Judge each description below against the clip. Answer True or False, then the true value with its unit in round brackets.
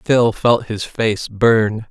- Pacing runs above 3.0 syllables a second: False (2.7 syllables/s)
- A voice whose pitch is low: True (110 Hz)